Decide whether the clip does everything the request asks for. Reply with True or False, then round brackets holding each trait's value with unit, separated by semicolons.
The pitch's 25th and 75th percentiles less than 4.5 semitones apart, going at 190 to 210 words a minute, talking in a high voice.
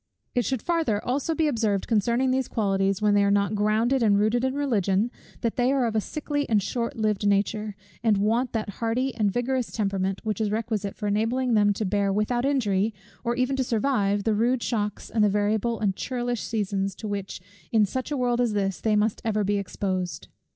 True (3.1 semitones; 205 wpm; 215 Hz)